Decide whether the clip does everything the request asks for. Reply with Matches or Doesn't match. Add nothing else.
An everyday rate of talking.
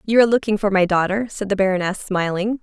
Doesn't match